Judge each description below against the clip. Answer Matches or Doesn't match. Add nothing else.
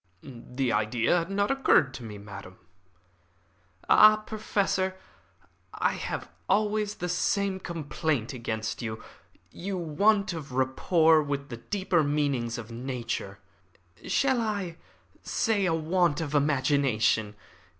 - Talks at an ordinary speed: Doesn't match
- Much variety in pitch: Matches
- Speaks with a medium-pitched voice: Matches